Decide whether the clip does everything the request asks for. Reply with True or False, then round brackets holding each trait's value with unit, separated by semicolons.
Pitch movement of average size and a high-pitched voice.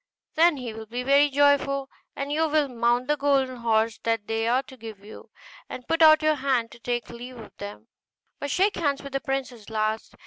True (3.8 semitones; 255 Hz)